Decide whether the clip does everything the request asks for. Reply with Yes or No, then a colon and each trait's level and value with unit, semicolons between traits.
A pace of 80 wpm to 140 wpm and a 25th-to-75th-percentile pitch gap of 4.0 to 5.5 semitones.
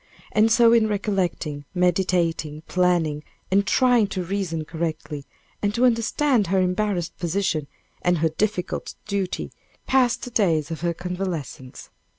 Yes: slow, 135 wpm; average, 4.3 semitones